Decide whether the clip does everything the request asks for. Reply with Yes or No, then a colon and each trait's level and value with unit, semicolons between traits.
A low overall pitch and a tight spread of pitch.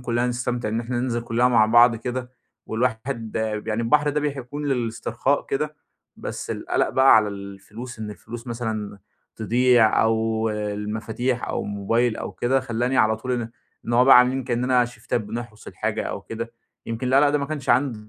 Yes: low, 120 Hz; narrow, 2.3 semitones